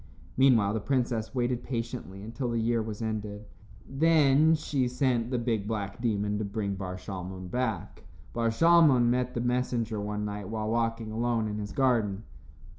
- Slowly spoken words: No, average, 165 wpm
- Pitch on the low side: Yes, low, 115 Hz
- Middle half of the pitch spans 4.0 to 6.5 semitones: No, average, 3.2 semitones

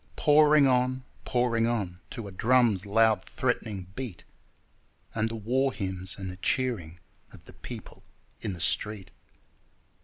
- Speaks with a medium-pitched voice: No, low, 115 Hz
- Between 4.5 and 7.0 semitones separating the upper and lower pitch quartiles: Yes, average, 4.9 semitones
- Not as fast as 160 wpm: Yes, average, 140 wpm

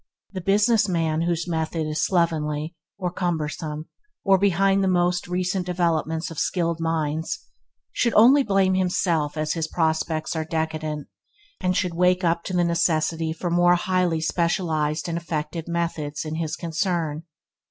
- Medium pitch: Yes, medium, 170 Hz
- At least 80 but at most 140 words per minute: No, average, 150 wpm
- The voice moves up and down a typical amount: No, narrow, 2.3 semitones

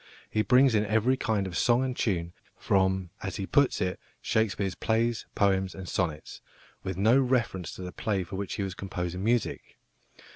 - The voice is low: Yes, low, 100 Hz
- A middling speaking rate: Yes, average, 180 wpm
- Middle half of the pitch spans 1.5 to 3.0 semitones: No, average, 3.4 semitones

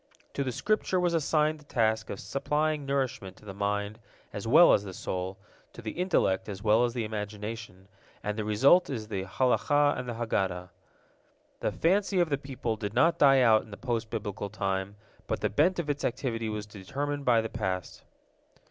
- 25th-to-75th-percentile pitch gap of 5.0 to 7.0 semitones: Yes, wide, 5.6 semitones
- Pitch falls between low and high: No, low, 115 Hz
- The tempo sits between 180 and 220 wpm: Yes, average, 195 wpm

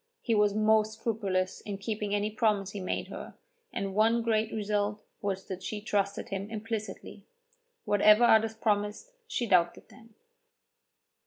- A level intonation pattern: Yes, narrow, 1.6 semitones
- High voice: Yes, high, 210 Hz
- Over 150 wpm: No, average, 145 wpm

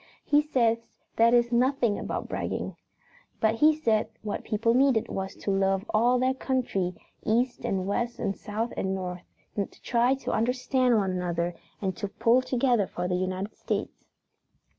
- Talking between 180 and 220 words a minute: No, average, 160 wpm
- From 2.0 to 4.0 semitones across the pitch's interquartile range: No, average, 4.5 semitones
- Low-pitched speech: No, high, 225 Hz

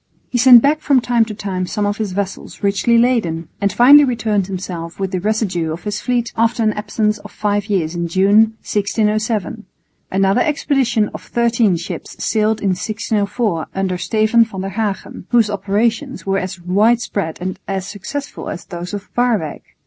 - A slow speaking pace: No, average, 170 wpm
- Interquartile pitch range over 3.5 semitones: No, average, 3.2 semitones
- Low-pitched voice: No, high, 210 Hz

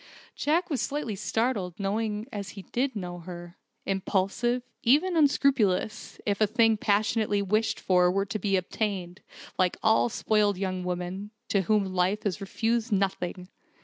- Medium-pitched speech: No, high, 205 Hz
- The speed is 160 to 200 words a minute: No, average, 150 wpm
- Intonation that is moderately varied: Yes, average, 3.3 semitones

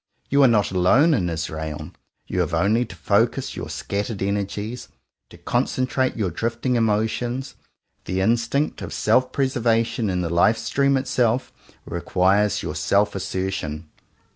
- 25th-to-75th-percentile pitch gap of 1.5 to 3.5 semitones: No, average, 4.9 semitones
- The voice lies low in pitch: Yes, low, 105 Hz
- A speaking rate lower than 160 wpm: Yes, average, 140 wpm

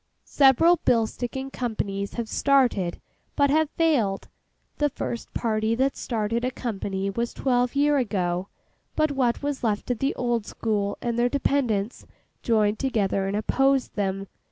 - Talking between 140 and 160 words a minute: Yes, average, 150 wpm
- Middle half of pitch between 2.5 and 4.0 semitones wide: No, average, 4.6 semitones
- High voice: Yes, high, 235 Hz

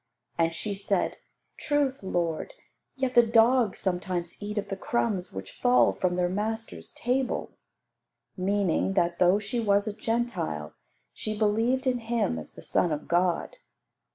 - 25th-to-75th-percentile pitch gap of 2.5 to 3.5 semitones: No, average, 4.7 semitones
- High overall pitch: Yes, high, 205 Hz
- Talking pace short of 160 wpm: Yes, average, 150 wpm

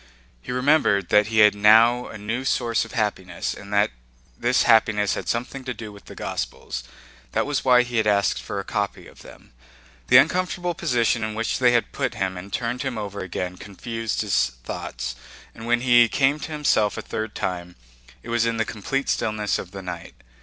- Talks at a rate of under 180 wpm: No, average, 195 wpm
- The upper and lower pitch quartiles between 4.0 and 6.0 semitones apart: No, average, 3.2 semitones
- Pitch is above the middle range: No, low, 110 Hz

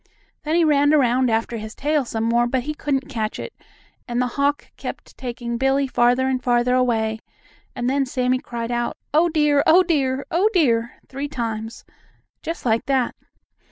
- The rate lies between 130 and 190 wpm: Yes, average, 175 wpm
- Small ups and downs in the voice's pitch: No, average, 3.2 semitones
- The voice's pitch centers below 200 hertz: No, very high, 255 Hz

